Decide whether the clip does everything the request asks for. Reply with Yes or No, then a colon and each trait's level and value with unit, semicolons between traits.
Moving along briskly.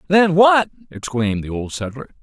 No: average, 160 wpm